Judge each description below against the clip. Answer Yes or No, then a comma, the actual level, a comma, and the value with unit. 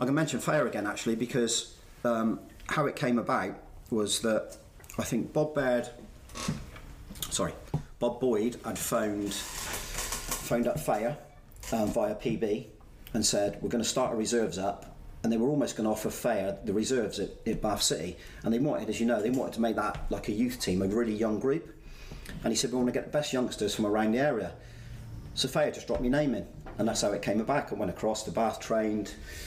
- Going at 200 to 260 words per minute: Yes, fast, 205 wpm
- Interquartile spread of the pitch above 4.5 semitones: No, narrow, 2.4 semitones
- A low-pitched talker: Yes, low, 115 Hz